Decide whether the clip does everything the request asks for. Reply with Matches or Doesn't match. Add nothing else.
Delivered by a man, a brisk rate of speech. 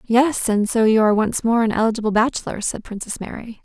Doesn't match